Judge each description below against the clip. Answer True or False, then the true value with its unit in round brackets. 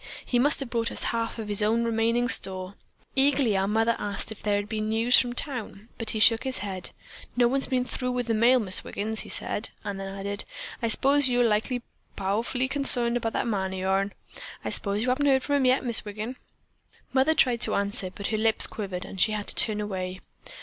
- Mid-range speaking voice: False (225 Hz)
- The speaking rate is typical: False (220 wpm)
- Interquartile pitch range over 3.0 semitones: True (3.5 semitones)